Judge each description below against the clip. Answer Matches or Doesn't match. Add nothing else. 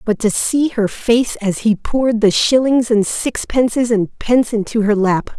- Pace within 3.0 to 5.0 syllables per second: Matches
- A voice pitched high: Matches